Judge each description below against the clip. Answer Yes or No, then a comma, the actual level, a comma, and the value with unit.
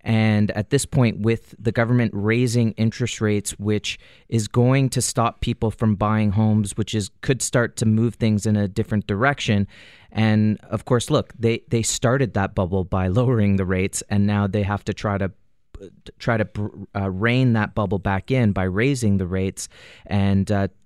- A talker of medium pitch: No, low, 105 Hz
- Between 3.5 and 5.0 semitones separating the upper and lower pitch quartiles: No, narrow, 2.5 semitones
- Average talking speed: Yes, average, 185 wpm